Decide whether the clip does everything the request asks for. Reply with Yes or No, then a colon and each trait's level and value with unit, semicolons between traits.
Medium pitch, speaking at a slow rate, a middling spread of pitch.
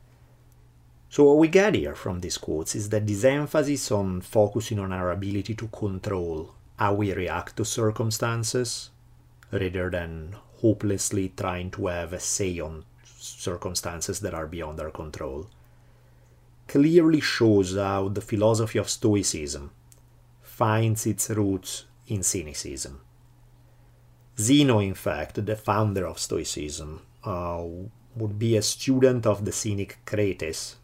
No: low, 105 Hz; slow, 130 wpm; average, 4.3 semitones